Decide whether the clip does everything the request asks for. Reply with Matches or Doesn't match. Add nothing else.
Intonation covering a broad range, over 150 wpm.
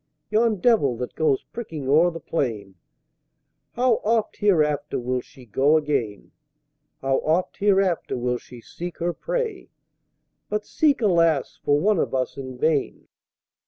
Doesn't match